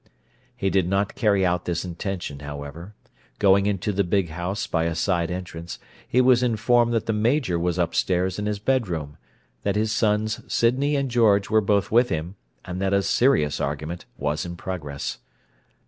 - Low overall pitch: Yes, very low, 95 Hz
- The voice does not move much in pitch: No, average, 4.1 semitones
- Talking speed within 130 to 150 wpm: No, average, 175 wpm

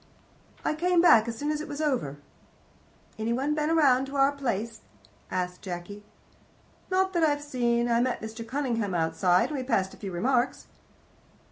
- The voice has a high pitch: Yes, high, 245 Hz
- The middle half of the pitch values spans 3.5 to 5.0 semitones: No, wide, 5.5 semitones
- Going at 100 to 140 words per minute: No, average, 170 wpm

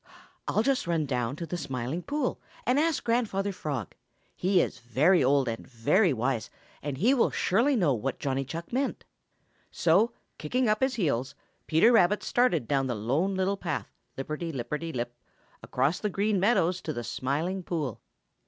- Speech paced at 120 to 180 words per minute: Yes, average, 170 wpm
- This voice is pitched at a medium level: Yes, medium, 165 Hz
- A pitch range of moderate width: No, wide, 7.2 semitones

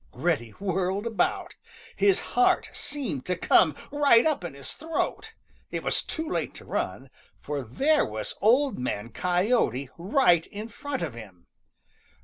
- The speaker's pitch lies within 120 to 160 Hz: No, high, 190 Hz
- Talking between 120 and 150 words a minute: Yes, average, 145 wpm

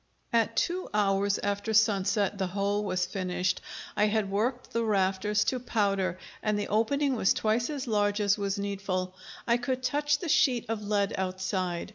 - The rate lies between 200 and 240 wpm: No, average, 170 wpm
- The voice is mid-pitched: No, high, 205 Hz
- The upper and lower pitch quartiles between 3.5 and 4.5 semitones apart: No, average, 2.7 semitones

